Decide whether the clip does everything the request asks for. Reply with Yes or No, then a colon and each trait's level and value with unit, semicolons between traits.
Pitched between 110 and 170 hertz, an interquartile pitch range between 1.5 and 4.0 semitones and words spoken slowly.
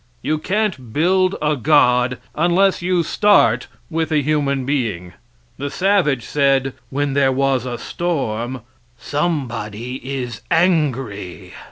No: medium, 140 Hz; average, 4.7 semitones; slow, 120 wpm